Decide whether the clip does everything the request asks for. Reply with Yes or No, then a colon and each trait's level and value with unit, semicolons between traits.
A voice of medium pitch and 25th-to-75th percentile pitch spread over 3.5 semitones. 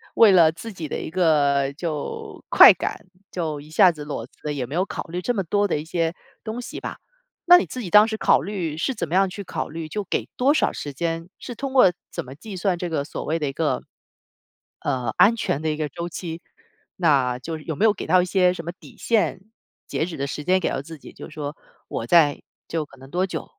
Yes: medium, 165 Hz; average, 3.9 semitones